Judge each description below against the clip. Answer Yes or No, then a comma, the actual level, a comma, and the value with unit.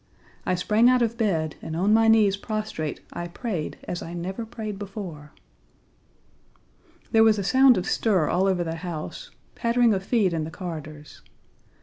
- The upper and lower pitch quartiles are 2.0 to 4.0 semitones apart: No, average, 4.6 semitones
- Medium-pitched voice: No, high, 195 Hz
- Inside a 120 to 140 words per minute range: No, average, 165 wpm